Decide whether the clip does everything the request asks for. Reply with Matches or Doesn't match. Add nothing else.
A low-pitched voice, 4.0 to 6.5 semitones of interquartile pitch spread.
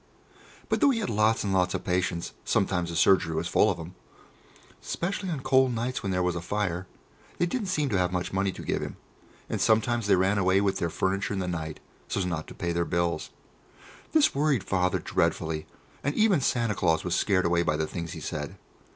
Matches